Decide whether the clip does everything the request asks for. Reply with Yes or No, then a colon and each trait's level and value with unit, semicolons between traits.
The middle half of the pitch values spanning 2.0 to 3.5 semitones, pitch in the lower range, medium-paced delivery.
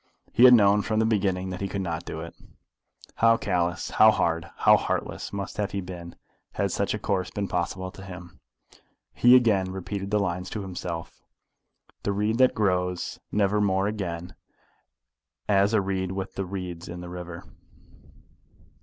Yes: narrow, 2.5 semitones; very low, 95 Hz; average, 170 wpm